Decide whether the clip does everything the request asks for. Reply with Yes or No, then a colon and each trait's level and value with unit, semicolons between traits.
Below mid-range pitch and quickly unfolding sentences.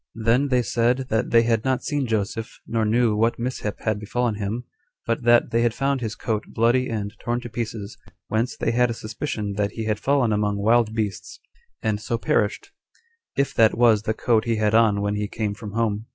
Yes: low, 115 Hz; fast, 210 wpm